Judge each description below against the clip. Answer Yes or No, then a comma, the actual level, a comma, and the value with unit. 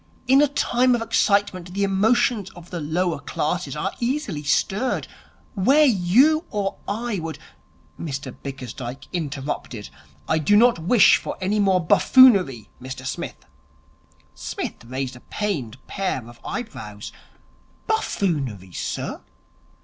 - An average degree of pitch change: No, wide, 8.3 semitones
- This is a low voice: No, medium, 185 Hz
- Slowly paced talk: Yes, slow, 130 wpm